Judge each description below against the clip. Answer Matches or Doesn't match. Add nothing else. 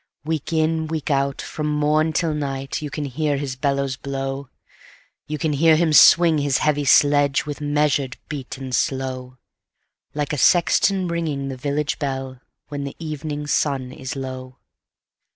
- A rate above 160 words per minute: Doesn't match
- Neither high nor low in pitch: Matches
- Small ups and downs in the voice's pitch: Matches